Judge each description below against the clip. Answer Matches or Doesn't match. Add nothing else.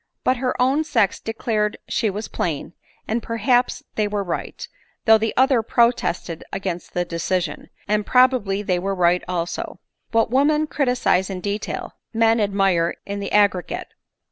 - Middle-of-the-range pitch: Doesn't match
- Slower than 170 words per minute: Matches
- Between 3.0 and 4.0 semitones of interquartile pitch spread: Doesn't match